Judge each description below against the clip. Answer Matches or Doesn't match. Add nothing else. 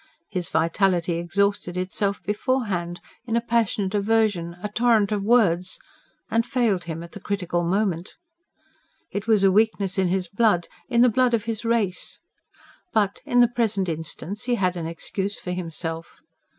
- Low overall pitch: Doesn't match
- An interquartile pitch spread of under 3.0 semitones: Doesn't match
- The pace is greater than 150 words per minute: Matches